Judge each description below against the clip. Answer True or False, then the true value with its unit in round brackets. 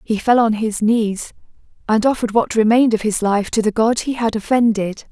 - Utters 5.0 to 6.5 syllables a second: True (5.4 syllables/s)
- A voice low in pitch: False (220 Hz)